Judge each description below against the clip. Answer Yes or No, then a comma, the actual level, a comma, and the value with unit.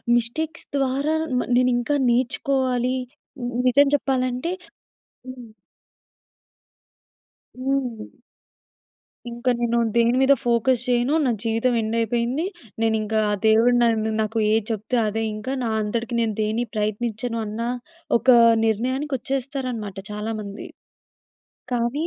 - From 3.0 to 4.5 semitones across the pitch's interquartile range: No, narrow, 2.5 semitones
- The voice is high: Yes, high, 240 Hz